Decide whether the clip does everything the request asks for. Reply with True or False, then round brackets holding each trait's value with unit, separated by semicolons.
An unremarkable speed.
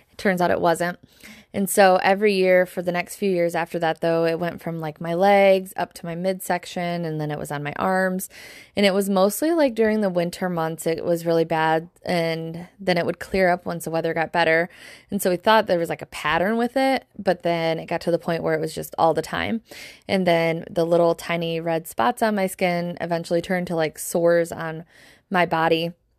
False (230 wpm)